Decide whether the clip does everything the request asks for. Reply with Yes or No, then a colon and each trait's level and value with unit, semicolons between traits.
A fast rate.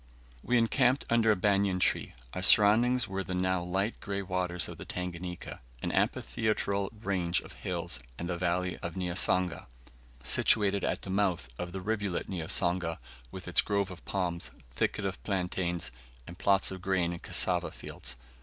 No: average, 165 wpm